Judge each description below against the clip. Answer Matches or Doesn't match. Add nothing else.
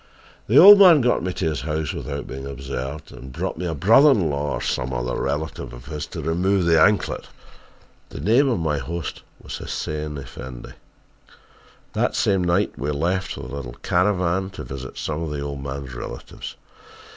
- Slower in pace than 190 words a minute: Matches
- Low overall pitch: Matches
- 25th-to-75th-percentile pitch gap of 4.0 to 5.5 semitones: Matches